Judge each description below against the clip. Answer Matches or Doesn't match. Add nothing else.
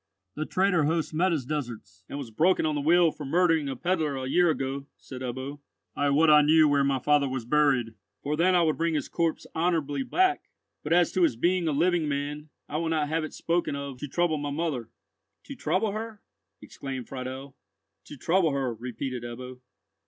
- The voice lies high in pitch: Doesn't match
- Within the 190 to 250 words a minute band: Matches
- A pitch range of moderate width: Matches